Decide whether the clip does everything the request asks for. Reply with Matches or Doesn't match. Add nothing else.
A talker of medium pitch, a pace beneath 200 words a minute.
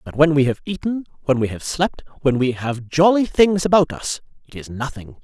Doesn't match